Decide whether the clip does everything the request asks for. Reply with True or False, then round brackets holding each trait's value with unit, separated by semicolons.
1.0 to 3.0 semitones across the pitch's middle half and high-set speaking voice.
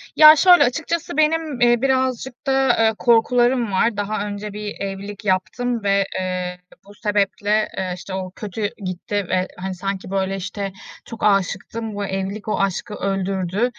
False (3.8 semitones; 205 Hz)